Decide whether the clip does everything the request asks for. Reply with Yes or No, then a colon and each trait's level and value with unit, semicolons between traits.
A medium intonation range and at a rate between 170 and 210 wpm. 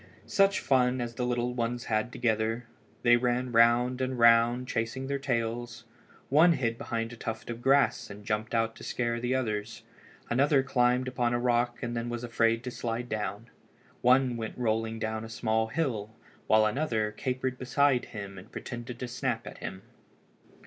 No: narrow, 1.9 semitones; average, 175 wpm